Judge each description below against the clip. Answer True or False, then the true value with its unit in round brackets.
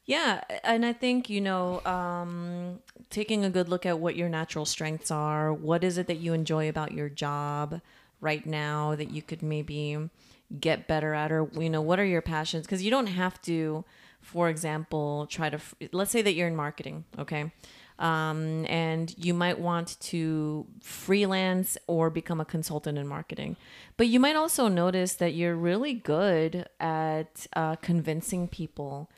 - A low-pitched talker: False (165 Hz)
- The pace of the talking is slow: False (175 wpm)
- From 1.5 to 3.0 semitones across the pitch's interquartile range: True (2.7 semitones)